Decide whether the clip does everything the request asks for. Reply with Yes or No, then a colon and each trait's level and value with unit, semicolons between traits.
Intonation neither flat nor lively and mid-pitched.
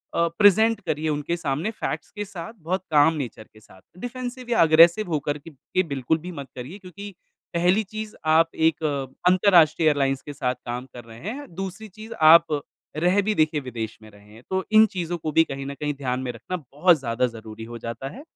No: wide, 5.7 semitones; medium, 160 Hz